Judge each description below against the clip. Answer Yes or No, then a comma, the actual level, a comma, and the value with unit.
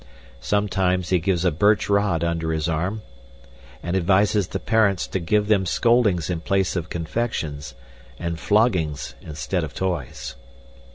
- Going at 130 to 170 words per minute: Yes, average, 140 wpm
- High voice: No, very low, 90 Hz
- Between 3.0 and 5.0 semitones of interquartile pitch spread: Yes, average, 3.7 semitones